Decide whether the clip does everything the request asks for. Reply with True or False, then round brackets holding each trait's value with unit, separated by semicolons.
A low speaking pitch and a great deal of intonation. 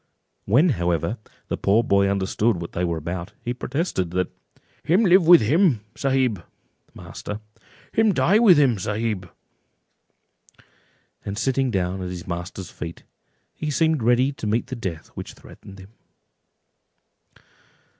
True (110 Hz; 6.9 semitones)